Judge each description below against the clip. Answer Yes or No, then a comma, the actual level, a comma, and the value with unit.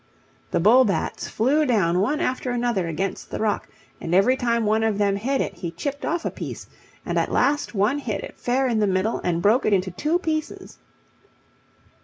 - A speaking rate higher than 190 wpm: Yes, average, 200 wpm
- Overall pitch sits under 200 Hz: No, high, 225 Hz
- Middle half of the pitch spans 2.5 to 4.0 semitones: No, average, 5.1 semitones